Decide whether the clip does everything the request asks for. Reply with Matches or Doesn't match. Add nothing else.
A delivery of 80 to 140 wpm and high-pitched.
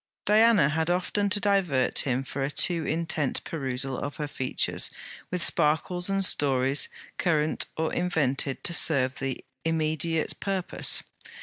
Doesn't match